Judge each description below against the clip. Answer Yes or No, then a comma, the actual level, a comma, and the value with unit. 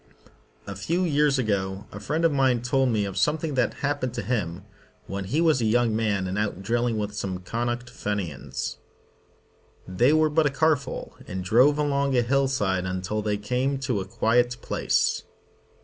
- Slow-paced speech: No, average, 180 wpm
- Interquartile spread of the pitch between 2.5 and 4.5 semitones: No, wide, 5.4 semitones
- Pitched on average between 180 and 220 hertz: No, low, 120 Hz